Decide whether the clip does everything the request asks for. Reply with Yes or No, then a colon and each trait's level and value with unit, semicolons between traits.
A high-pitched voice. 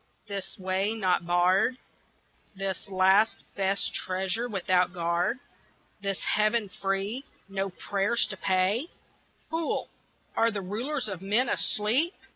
Yes: high, 195 Hz